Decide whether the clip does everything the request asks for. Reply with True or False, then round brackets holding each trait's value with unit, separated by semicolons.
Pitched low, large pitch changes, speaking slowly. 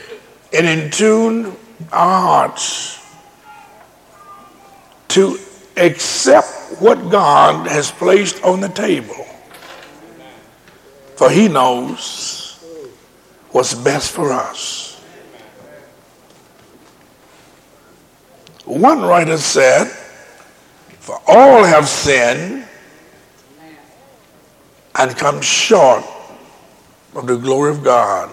False (190 Hz; 6.0 semitones; 75 wpm)